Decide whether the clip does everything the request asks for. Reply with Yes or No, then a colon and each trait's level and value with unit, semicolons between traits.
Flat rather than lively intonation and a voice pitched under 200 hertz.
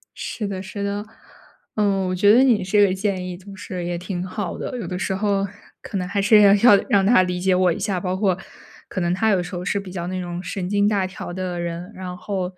Yes: narrow, 2.0 semitones; high, 190 Hz